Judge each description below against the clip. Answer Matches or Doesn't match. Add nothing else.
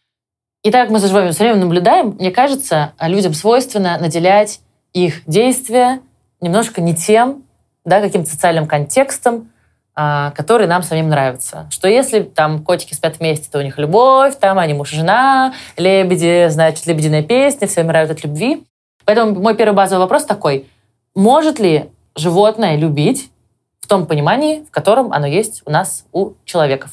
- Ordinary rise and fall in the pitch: Doesn't match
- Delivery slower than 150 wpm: Doesn't match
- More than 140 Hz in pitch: Matches